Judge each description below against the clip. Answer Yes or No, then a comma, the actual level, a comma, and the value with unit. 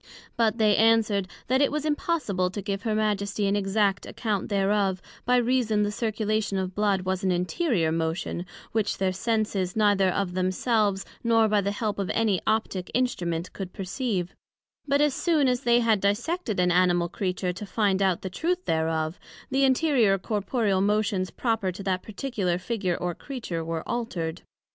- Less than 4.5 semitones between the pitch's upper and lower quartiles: Yes, average, 3.5 semitones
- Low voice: No, high, 205 Hz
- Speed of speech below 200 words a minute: Yes, average, 170 wpm